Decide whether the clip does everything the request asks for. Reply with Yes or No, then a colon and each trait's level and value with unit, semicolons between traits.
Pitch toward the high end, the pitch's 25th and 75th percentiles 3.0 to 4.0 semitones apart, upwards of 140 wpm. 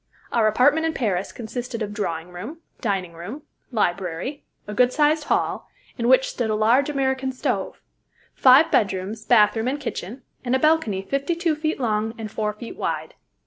No: high, 235 Hz; average, 4.7 semitones; average, 170 wpm